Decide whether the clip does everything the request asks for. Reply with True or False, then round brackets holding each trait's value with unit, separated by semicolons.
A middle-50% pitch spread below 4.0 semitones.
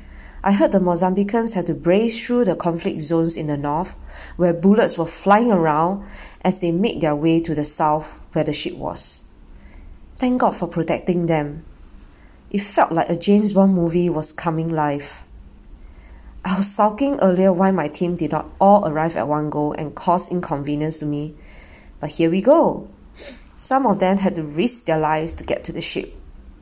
False (4.4 semitones)